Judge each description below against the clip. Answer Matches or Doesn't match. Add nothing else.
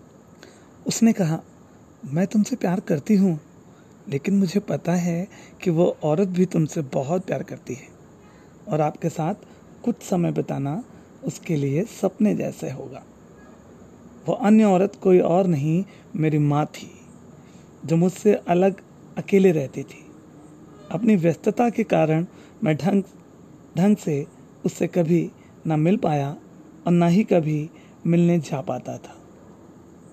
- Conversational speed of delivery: Matches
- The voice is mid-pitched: Matches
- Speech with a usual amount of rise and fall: Matches